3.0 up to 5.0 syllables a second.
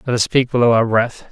No: 6.0 syllables/s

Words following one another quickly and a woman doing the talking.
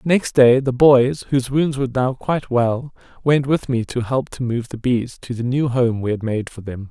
No: fast, 245 wpm; male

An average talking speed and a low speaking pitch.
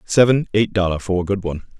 Yes: average, 165 wpm; low, 100 Hz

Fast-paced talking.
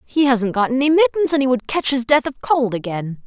Yes: fast, 255 wpm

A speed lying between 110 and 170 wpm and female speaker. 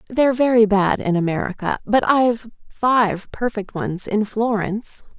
Yes: average, 140 wpm; female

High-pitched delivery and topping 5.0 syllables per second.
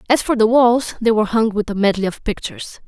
Yes: high, 225 Hz; 6.1 syllables/s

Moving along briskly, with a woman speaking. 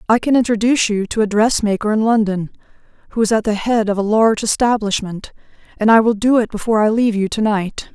Yes: fast, 220 wpm; female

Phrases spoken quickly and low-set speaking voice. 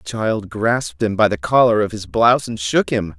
Yes: fast, 245 wpm; low, 105 Hz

